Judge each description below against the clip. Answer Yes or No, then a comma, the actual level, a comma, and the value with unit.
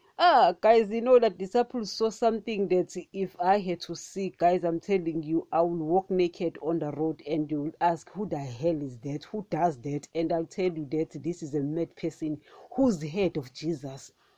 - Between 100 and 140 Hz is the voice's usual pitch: No, medium, 170 Hz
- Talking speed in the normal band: No, fast, 215 wpm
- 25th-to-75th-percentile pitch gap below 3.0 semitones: No, average, 3.4 semitones